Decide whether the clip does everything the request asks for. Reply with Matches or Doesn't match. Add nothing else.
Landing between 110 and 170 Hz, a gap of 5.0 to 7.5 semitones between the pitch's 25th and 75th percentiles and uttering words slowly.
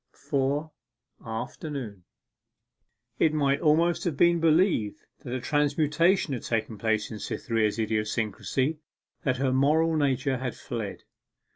Matches